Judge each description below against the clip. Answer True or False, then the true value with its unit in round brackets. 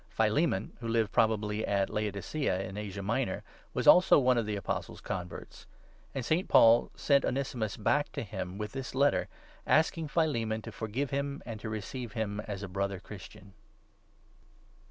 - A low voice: True (110 Hz)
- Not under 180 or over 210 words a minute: False (160 wpm)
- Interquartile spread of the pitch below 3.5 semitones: False (4.7 semitones)